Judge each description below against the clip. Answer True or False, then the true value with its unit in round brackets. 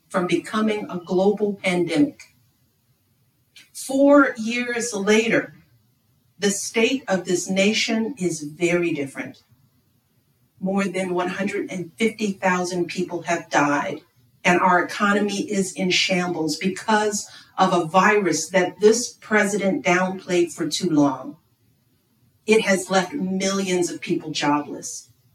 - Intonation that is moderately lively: False (5.7 semitones)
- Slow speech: True (110 wpm)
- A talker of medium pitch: True (180 Hz)